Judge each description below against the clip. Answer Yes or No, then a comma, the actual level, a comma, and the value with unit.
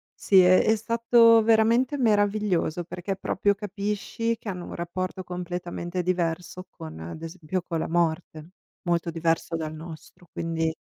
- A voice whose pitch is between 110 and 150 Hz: No, medium, 180 Hz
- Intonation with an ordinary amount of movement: Yes, average, 3.8 semitones